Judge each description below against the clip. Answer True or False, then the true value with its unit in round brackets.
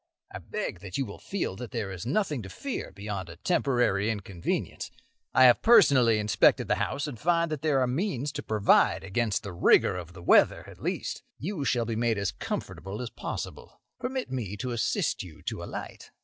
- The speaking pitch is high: False (120 Hz)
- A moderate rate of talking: True (195 wpm)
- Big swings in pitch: True (6.2 semitones)